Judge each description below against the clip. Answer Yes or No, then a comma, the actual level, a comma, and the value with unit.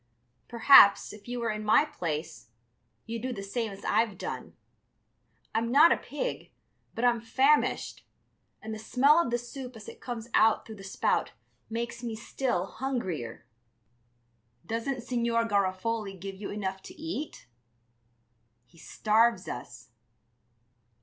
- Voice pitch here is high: Yes, high, 225 Hz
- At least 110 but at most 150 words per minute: Yes, average, 140 wpm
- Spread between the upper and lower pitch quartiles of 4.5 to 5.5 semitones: No, average, 3.6 semitones